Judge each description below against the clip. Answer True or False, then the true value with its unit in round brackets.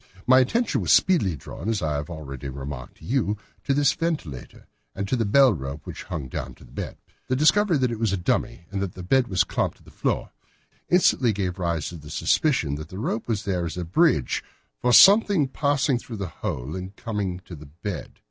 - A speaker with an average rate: False (220 wpm)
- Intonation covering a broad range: True (8.4 semitones)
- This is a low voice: True (100 Hz)